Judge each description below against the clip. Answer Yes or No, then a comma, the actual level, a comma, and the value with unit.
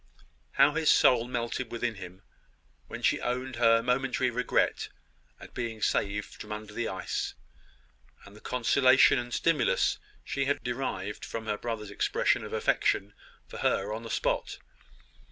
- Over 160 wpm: No, average, 150 wpm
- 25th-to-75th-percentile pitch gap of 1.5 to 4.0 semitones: Yes, average, 3.1 semitones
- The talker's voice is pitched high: No, low, 120 Hz